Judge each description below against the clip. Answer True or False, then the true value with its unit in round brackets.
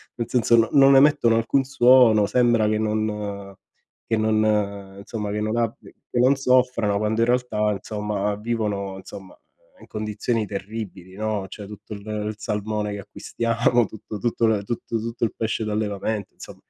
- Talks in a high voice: False (110 Hz)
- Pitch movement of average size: False (1.9 semitones)